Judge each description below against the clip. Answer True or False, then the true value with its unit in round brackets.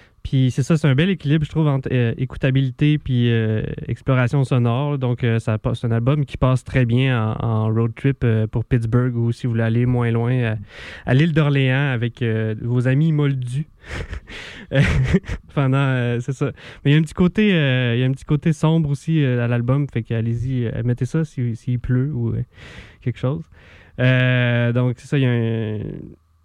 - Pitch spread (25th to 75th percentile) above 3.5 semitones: False (3.1 semitones)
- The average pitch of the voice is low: True (125 Hz)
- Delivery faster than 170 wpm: True (210 wpm)